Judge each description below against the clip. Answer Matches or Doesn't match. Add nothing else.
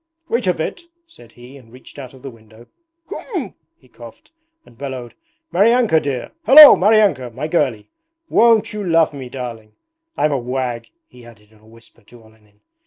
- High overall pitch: Doesn't match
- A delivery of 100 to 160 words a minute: Doesn't match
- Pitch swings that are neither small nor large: Doesn't match